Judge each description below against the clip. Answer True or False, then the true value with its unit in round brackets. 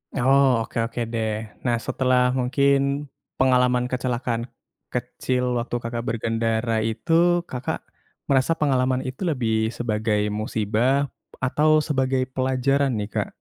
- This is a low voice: True (125 Hz)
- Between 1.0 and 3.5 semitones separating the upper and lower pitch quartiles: True (2.9 semitones)